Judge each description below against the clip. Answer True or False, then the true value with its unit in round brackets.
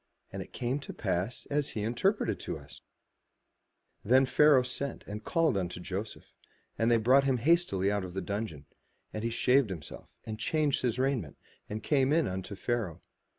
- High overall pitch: False (115 Hz)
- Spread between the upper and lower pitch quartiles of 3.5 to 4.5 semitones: False (5.4 semitones)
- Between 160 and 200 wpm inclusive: True (170 wpm)